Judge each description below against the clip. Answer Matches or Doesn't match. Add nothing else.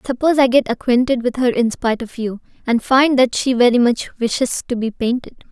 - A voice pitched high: Matches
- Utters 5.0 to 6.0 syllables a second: Matches